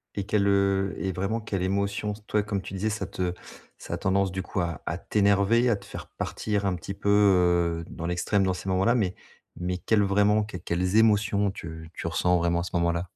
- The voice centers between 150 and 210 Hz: No, very low, 95 Hz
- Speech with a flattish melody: Yes, narrow, 2.3 semitones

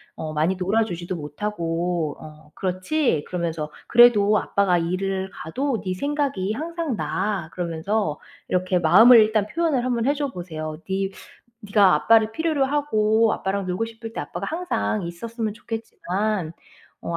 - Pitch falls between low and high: No, high, 200 Hz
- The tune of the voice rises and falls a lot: No, average, 4.9 semitones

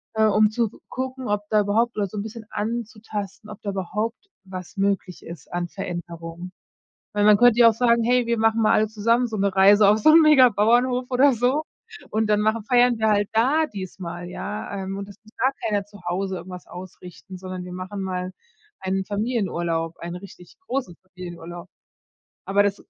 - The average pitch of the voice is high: Yes, high, 205 Hz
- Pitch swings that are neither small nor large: Yes, average, 3.6 semitones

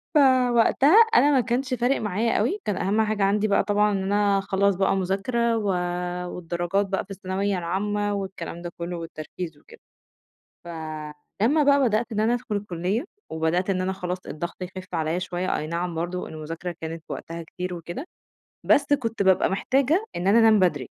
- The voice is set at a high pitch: Yes, high, 195 Hz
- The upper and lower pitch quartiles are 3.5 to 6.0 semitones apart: Yes, average, 4.2 semitones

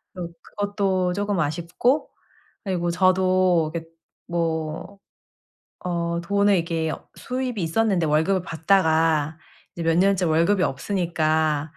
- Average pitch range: Yes, average, 3.2 semitones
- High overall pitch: No, medium, 175 Hz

